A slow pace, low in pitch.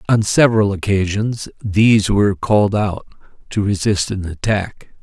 Yes: slow, 130 wpm; low, 100 Hz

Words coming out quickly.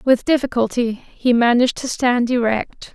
No: average, 145 wpm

